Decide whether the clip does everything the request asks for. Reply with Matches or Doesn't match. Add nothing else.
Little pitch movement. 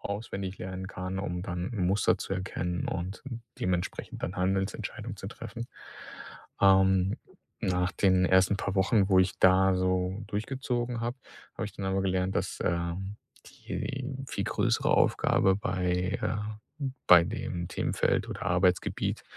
Matches